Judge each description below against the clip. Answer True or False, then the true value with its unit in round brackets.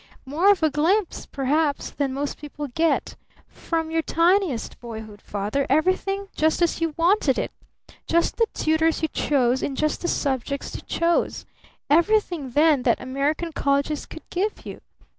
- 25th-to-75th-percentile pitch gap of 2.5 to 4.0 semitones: True (3.5 semitones)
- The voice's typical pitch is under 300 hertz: False (310 Hz)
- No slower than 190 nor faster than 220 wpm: False (155 wpm)